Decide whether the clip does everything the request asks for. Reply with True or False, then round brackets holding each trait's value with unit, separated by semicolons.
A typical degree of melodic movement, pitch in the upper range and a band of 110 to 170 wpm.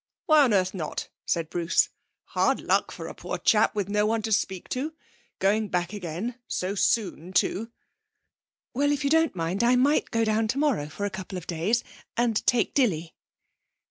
False (4.9 semitones; 210 Hz; 180 wpm)